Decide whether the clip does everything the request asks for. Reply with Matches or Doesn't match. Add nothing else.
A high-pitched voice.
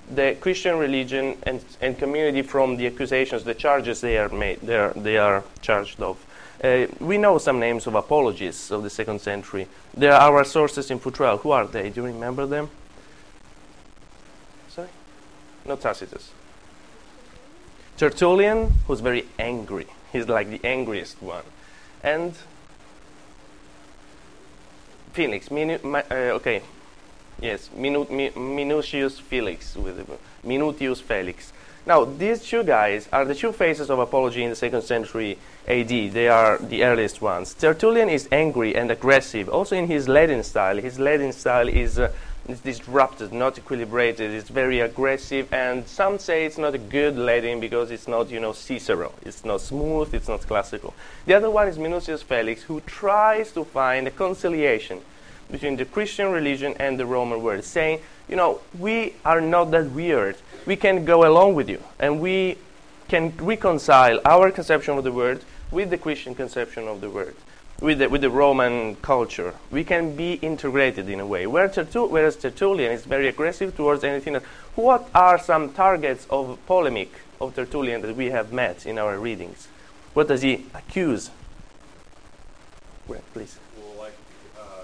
Doesn't match